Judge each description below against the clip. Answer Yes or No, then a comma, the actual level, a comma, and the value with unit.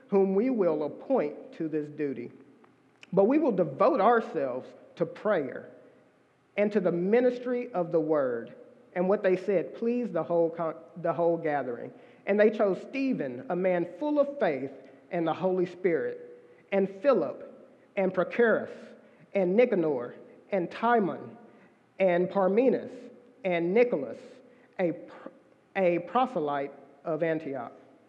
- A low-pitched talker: No, high, 190 Hz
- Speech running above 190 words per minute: No, slow, 135 wpm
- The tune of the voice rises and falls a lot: Yes, wide, 6.6 semitones